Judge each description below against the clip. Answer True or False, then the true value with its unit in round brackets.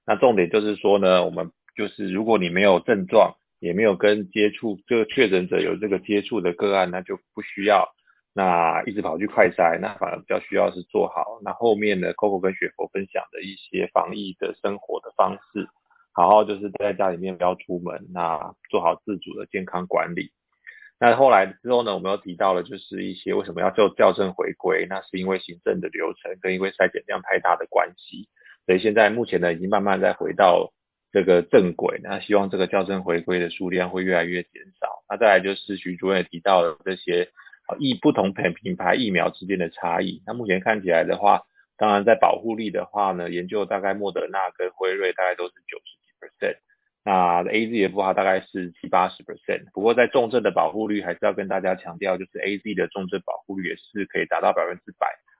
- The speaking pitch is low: True (95 Hz)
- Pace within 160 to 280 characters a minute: False (335 characters per minute)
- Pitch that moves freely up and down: False (2.6 semitones)